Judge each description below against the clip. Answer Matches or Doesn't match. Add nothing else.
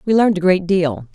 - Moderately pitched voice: Matches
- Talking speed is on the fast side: Matches